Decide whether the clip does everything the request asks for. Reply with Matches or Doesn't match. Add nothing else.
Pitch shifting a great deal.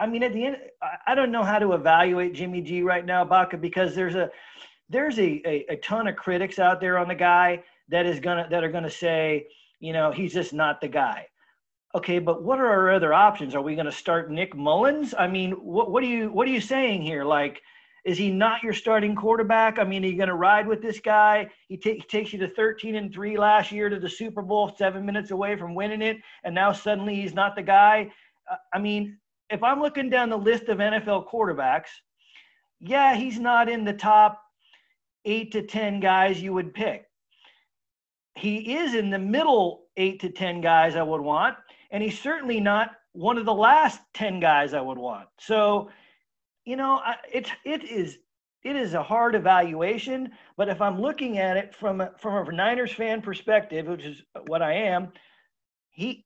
Doesn't match